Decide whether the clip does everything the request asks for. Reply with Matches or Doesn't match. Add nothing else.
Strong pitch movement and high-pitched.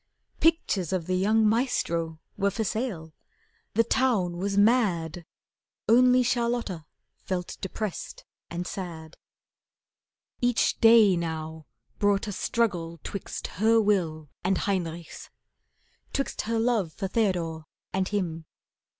Doesn't match